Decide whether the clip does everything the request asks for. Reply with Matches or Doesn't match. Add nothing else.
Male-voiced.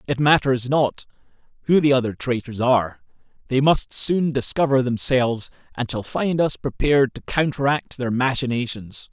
Matches